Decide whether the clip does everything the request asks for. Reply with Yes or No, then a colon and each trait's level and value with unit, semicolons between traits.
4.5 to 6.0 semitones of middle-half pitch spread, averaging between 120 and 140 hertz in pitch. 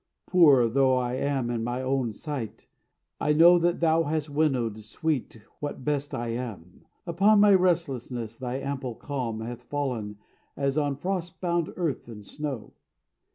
Yes: average, 4.8 semitones; low, 135 Hz